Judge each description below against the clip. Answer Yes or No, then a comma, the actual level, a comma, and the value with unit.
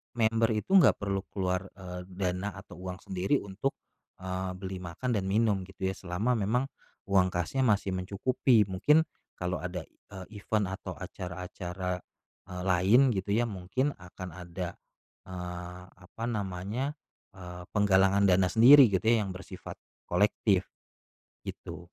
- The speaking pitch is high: No, very low, 95 Hz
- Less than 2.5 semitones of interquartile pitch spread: No, average, 2.8 semitones